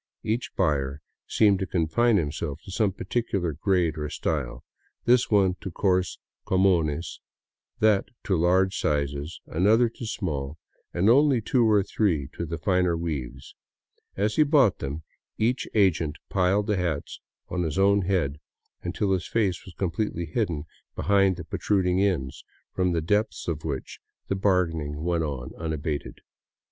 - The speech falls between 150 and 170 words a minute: Yes, average, 155 wpm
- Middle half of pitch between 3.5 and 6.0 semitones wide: Yes, average, 4.2 semitones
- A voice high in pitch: No, very low, 90 Hz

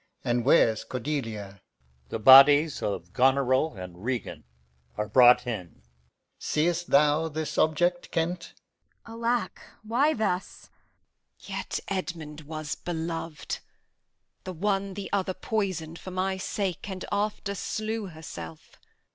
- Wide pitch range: Yes, wide, 6.5 semitones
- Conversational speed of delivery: No, slow, 120 wpm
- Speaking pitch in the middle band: Yes, medium, 160 Hz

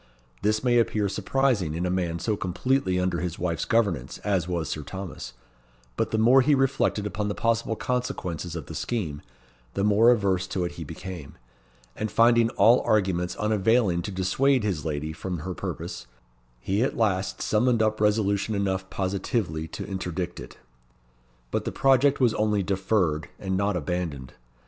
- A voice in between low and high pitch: No, very low, 95 Hz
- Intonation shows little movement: No, average, 3.9 semitones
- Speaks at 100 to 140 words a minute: No, average, 165 wpm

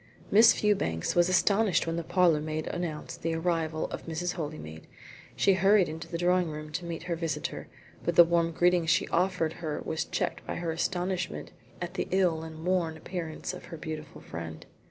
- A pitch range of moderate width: No, narrow, 2.2 semitones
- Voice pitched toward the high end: No, medium, 170 Hz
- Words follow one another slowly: No, average, 180 wpm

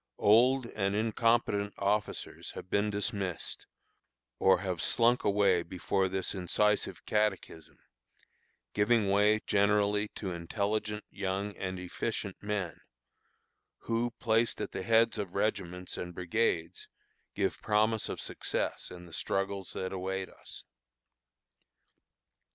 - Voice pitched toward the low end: Yes, low, 100 Hz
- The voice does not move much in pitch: Yes, narrow, 2.3 semitones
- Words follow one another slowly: Yes, slow, 115 wpm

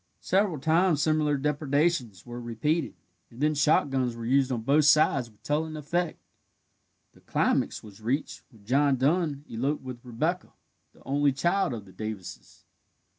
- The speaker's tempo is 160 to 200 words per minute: No, average, 150 wpm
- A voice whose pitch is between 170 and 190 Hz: No, medium, 140 Hz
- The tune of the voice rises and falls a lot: No, average, 4.3 semitones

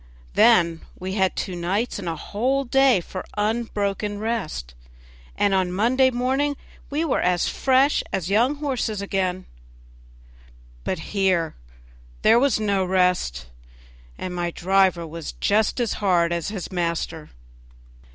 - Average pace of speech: No, slow, 130 wpm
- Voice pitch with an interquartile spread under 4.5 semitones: No, average, 4.8 semitones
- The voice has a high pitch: Yes, high, 195 Hz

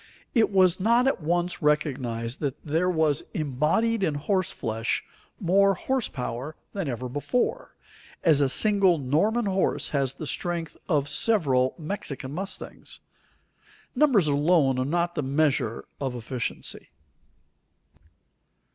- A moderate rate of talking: No, slow, 125 wpm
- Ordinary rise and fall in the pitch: No, wide, 5.8 semitones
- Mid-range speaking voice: Yes, medium, 155 Hz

